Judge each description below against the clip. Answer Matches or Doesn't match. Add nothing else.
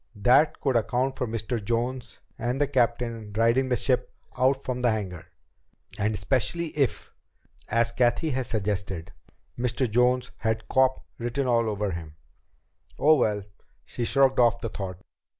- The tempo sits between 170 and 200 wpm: Doesn't match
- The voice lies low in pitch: Matches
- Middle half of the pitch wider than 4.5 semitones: Doesn't match